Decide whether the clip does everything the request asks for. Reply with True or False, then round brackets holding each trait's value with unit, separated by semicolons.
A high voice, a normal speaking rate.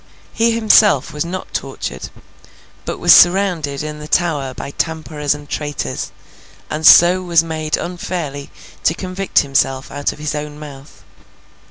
False (155 Hz; 145 wpm)